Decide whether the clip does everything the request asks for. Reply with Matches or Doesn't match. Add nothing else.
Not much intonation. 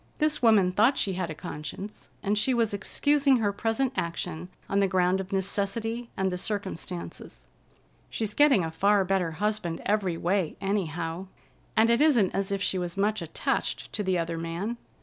Doesn't match